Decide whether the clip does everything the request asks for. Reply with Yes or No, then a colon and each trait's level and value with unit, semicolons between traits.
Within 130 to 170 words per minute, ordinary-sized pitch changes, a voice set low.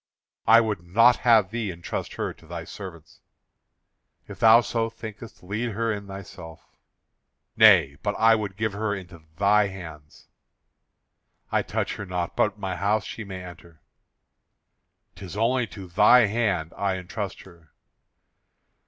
Yes: average, 145 wpm; average, 3.7 semitones; low, 100 Hz